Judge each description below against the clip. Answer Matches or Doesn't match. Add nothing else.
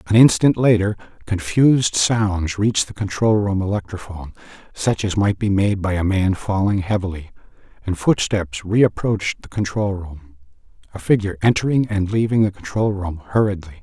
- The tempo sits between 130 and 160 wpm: Matches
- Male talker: Matches